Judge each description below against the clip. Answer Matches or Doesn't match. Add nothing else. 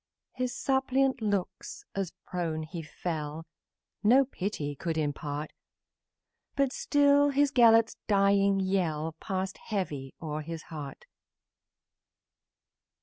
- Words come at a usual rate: Doesn't match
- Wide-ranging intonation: Matches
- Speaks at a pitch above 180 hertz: Matches